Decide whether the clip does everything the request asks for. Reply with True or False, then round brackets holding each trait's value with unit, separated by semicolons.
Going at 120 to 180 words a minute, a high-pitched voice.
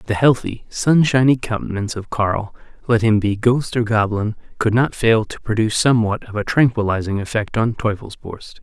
False (165 wpm; 110 Hz)